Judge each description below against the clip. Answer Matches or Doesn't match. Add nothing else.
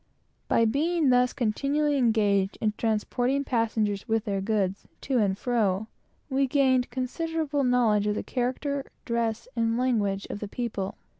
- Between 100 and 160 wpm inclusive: Matches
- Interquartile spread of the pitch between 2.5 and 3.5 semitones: Doesn't match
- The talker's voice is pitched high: Matches